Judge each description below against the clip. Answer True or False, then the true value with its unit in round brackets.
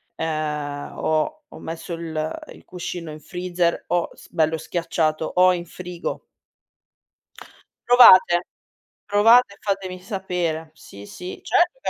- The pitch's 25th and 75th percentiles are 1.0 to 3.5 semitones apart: True (2.7 semitones)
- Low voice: False (175 Hz)